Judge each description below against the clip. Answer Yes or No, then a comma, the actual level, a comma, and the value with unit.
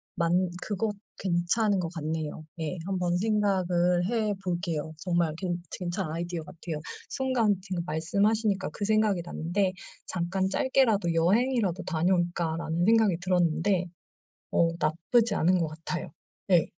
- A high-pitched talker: No, medium, 180 Hz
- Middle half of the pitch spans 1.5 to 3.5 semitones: Yes, average, 3.2 semitones